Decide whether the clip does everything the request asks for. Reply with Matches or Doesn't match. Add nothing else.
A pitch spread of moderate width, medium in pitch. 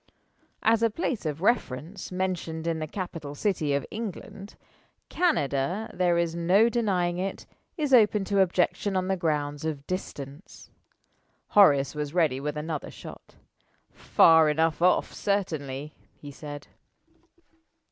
Matches